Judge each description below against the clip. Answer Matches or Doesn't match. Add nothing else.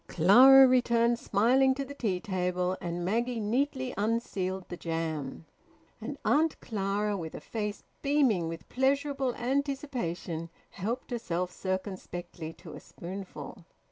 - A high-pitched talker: Matches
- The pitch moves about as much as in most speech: Doesn't match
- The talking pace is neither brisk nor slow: Doesn't match